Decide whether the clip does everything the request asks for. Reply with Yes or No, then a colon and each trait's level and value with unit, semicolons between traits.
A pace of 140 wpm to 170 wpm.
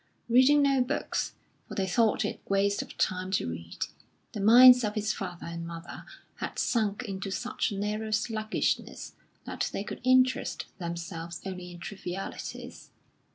Yes: average, 155 wpm